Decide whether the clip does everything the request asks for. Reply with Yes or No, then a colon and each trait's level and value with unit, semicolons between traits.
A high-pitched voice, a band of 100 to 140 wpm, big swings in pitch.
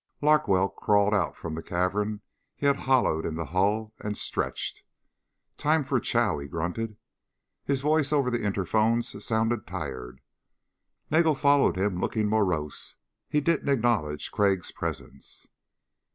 No: low, 105 Hz; slow, 135 wpm; wide, 6.4 semitones